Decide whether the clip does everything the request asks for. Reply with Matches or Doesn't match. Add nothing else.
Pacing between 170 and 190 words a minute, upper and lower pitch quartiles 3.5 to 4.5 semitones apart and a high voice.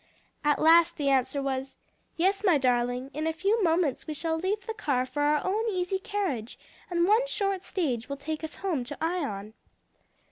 Doesn't match